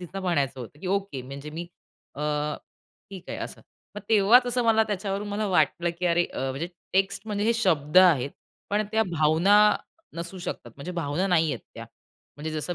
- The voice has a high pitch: No, medium, 180 Hz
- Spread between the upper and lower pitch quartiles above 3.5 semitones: Yes, average, 4.6 semitones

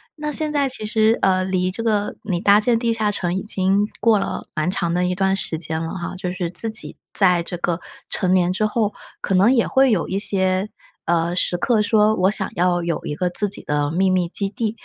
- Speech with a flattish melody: No, average, 3.2 semitones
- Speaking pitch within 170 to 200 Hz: Yes, high, 190 Hz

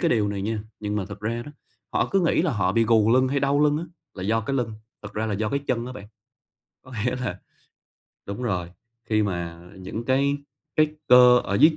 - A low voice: Yes, low, 115 Hz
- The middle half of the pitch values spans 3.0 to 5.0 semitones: Yes, average, 4.5 semitones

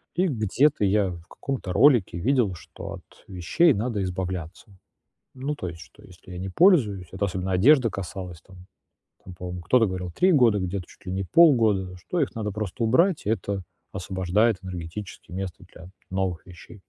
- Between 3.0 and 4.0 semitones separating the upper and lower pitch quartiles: No, average, 4.4 semitones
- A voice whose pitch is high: No, very low, 95 Hz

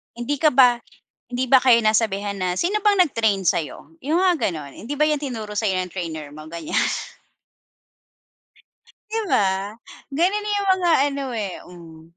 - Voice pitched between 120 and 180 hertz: No, high, 230 Hz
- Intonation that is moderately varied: No, wide, 8.4 semitones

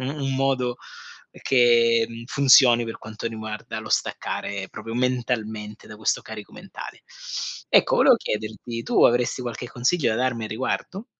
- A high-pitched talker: No, low, 115 Hz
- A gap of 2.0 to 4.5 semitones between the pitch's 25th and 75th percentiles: Yes, narrow, 2.6 semitones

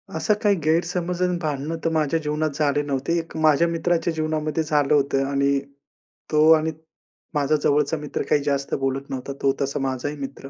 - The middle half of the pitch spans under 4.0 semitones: Yes, narrow, 2.5 semitones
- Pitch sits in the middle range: Yes, medium, 150 Hz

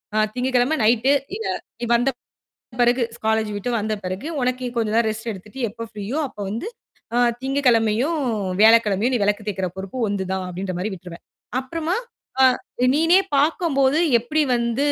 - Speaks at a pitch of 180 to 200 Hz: No, high, 235 Hz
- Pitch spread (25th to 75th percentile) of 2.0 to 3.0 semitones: No, average, 4.1 semitones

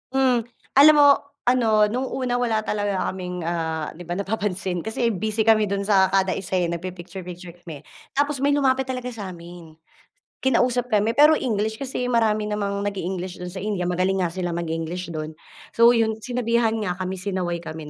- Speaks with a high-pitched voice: Yes, high, 200 Hz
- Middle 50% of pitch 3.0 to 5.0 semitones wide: Yes, average, 4.6 semitones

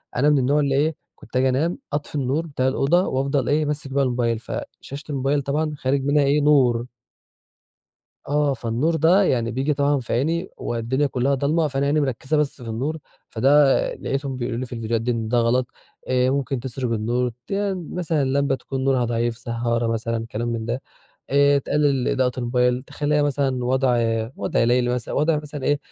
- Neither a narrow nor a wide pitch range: Yes, average, 3.0 semitones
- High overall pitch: No, low, 135 Hz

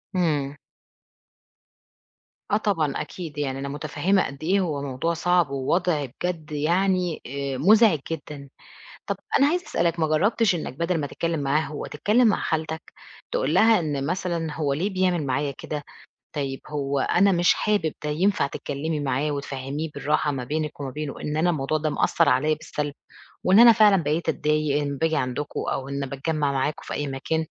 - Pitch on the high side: No, medium, 155 Hz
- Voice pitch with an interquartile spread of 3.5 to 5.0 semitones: Yes, average, 3.8 semitones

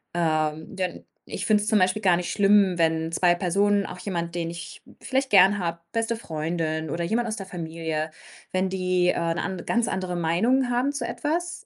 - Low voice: No, medium, 185 Hz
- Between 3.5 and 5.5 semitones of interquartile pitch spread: Yes, average, 4.3 semitones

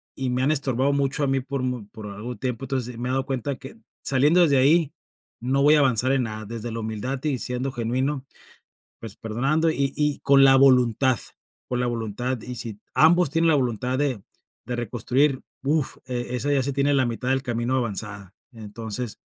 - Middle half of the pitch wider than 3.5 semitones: No, average, 2.7 semitones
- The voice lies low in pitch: Yes, low, 130 Hz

